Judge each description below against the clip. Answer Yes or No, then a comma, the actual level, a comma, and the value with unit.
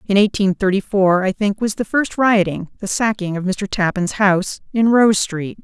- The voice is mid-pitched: No, high, 200 Hz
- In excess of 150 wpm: Yes, average, 200 wpm